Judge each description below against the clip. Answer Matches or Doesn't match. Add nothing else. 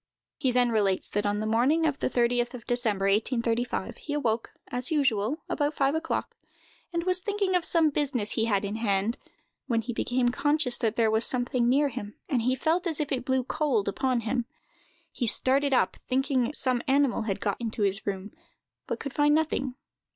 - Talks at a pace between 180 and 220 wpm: Matches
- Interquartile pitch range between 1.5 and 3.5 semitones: Doesn't match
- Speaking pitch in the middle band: Doesn't match